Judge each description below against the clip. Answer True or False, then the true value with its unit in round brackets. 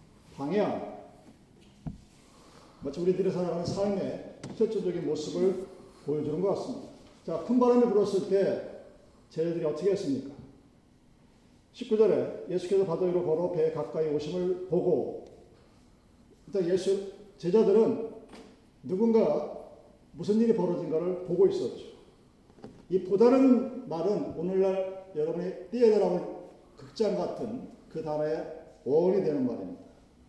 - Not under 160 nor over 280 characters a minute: True (260 characters per minute)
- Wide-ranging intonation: False (4.7 semitones)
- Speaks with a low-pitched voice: False (190 Hz)